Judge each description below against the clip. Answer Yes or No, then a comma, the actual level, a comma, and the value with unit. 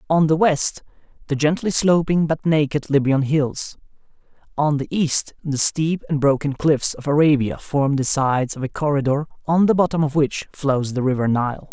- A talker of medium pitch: Yes, medium, 145 Hz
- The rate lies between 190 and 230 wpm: No, average, 180 wpm